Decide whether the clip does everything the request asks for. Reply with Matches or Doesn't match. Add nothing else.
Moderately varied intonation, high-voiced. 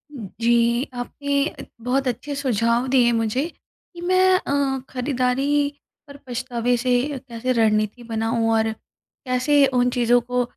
Matches